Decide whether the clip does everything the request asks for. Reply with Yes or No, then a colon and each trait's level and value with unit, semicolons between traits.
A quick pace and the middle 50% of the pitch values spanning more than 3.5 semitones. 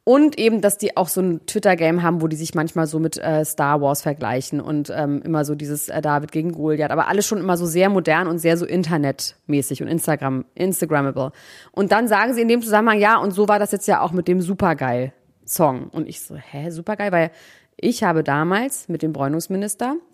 Yes: fast, 220 wpm; average, 5.1 semitones